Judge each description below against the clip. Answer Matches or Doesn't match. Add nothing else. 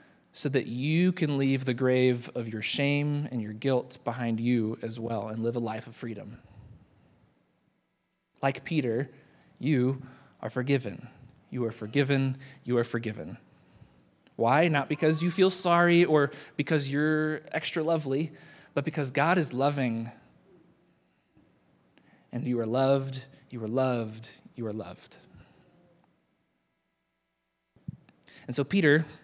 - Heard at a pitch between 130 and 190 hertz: Matches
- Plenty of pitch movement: Doesn't match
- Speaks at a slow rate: Matches